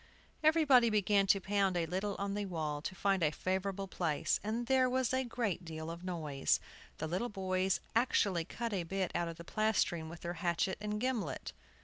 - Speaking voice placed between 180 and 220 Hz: Yes, high, 190 Hz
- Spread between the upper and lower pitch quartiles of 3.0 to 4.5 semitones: Yes, average, 3.9 semitones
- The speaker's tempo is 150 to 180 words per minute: No, average, 195 wpm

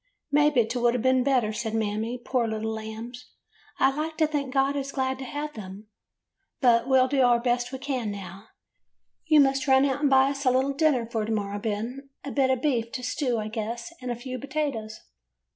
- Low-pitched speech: No, very high, 250 Hz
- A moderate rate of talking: No, fast, 225 wpm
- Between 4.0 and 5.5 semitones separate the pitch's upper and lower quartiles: No, average, 3.5 semitones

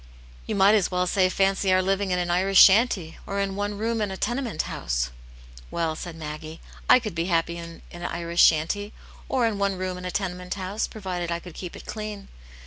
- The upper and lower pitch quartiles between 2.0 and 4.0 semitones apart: Yes, average, 2.9 semitones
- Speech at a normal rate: No, fast, 215 wpm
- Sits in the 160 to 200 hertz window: Yes, medium, 185 Hz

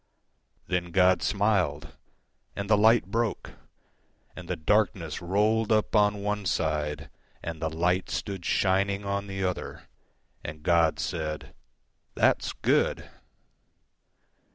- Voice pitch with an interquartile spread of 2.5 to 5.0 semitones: Yes, average, 3.9 semitones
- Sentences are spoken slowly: Yes, slow, 100 wpm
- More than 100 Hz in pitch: No, very low, 95 Hz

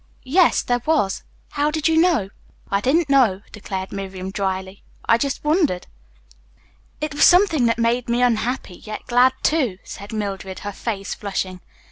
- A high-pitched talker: Yes, high, 235 Hz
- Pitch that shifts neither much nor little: No, wide, 7.0 semitones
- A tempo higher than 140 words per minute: Yes, average, 155 wpm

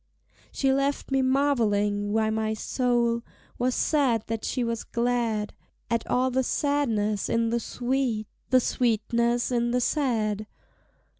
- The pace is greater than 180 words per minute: No, slow, 135 wpm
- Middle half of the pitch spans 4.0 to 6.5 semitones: No, average, 2.9 semitones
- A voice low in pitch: No, high, 235 Hz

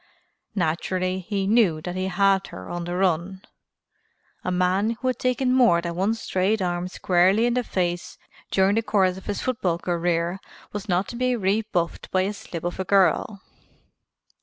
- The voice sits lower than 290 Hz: Yes, high, 190 Hz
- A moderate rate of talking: Yes, average, 175 wpm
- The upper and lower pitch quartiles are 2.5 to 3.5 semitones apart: Yes, average, 3.1 semitones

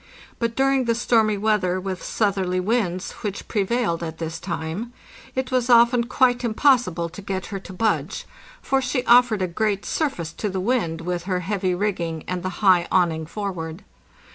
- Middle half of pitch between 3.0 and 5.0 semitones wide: Yes, average, 4.7 semitones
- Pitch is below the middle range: No, high, 195 Hz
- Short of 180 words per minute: Yes, average, 170 wpm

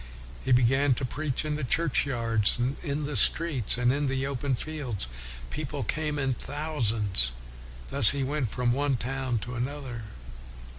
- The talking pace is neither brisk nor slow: Yes, average, 160 wpm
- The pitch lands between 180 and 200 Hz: No, low, 135 Hz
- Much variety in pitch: No, average, 3.2 semitones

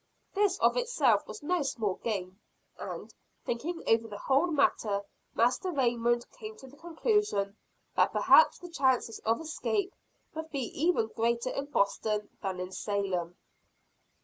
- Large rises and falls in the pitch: Yes, wide, 7.7 semitones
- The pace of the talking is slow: No, average, 145 wpm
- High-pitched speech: Yes, high, 245 Hz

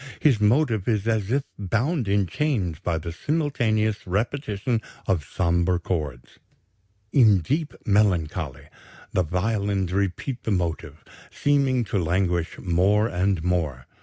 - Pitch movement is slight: No, average, 4.7 semitones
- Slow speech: Yes, slow, 125 wpm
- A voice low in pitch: Yes, low, 100 Hz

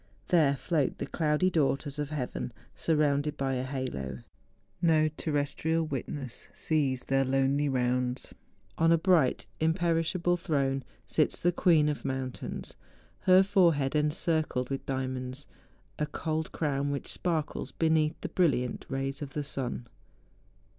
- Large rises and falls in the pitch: No, average, 3.2 semitones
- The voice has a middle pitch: Yes, medium, 145 Hz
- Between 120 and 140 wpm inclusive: Yes, slow, 135 wpm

